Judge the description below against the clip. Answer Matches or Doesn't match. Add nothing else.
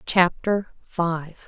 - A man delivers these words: Doesn't match